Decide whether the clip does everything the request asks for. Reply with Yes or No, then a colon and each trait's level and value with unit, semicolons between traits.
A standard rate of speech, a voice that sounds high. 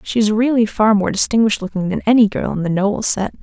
No: fast, 245 wpm; high, 210 Hz